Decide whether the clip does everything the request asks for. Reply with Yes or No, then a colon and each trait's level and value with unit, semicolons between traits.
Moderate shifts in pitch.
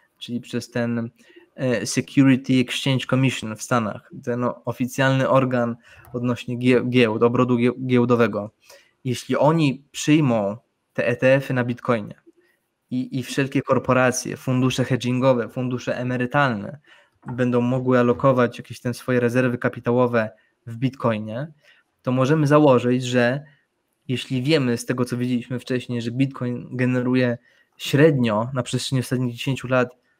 No: narrow, 1.4 semitones